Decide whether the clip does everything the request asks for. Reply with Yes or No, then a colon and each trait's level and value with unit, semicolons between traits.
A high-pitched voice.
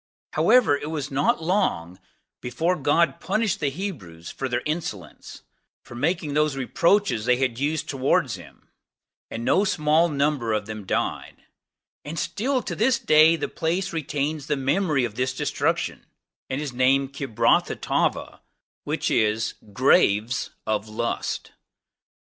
No: medium, 140 Hz